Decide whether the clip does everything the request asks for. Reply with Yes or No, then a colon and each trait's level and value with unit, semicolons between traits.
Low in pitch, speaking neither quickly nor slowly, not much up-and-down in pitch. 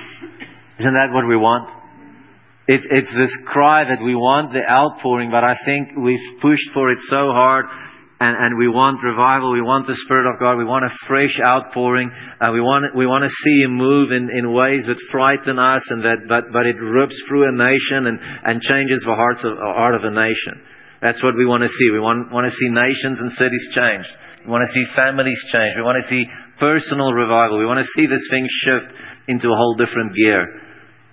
No: low, 125 Hz; fast, 220 wpm; narrow, 1.9 semitones